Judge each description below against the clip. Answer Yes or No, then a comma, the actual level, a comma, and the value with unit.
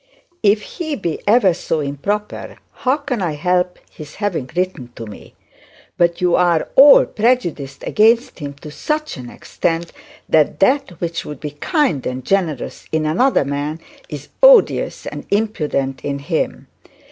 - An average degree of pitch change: No, wide, 6.4 semitones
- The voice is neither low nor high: Yes, medium, 170 Hz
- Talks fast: No, average, 150 wpm